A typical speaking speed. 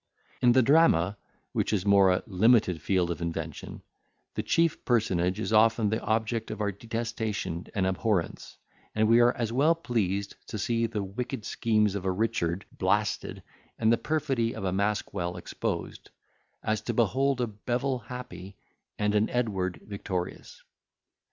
Yes: average, 155 wpm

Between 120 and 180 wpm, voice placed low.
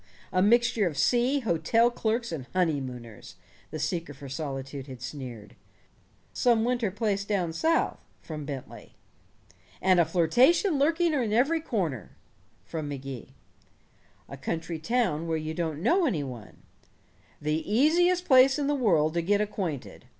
No: average, 145 wpm; medium, 175 Hz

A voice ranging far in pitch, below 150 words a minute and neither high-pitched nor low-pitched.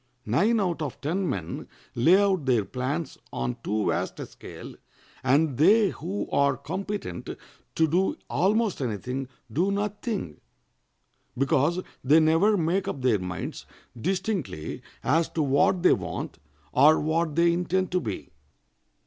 Yes: wide, 6.4 semitones; average, 140 wpm; medium, 160 Hz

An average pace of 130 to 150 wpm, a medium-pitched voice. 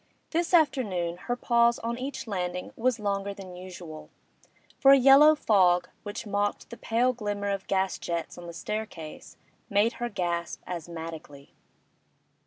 No: average, 145 wpm; high, 200 Hz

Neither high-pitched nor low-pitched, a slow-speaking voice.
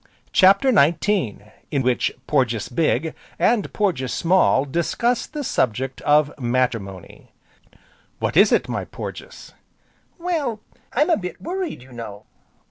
Yes: medium, 155 Hz; slow, 125 wpm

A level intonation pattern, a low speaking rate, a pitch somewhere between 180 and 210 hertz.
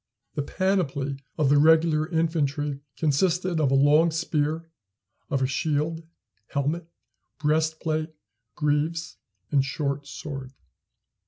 No: narrow, 2.2 semitones; slow, 105 wpm; medium, 155 Hz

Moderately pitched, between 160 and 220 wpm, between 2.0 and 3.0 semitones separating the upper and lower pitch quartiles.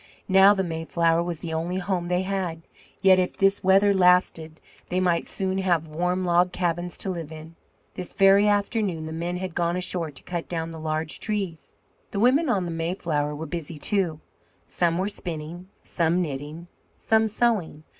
Yes: medium, 175 Hz; average, 175 wpm; average, 2.7 semitones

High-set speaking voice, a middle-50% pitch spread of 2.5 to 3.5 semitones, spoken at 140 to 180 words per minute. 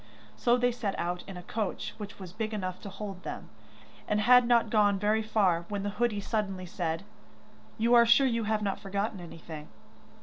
No: high, 205 Hz; average, 3.1 semitones; average, 195 wpm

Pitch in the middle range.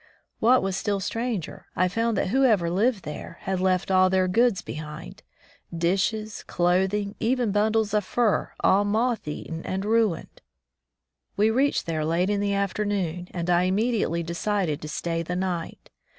No: high, 195 Hz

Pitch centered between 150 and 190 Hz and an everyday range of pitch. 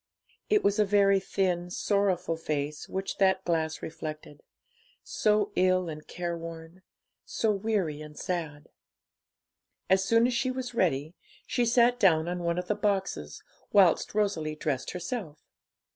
Yes: medium, 185 Hz; average, 4.2 semitones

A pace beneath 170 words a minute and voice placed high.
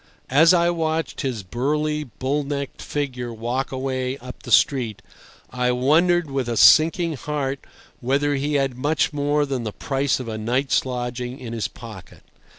No: average, 160 wpm; low, 135 Hz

